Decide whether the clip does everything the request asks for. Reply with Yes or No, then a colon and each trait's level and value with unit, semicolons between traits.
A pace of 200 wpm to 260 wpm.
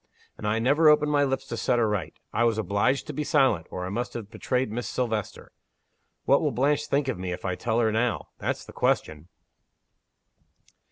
Yes: fast, 205 wpm